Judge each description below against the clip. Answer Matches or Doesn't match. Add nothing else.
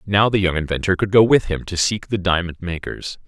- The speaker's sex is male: Matches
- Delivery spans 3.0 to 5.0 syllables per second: Doesn't match